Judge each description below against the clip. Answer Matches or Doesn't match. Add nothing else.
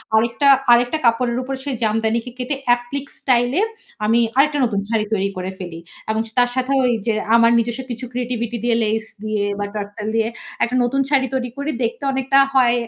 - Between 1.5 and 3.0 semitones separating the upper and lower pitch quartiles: Matches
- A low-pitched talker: Doesn't match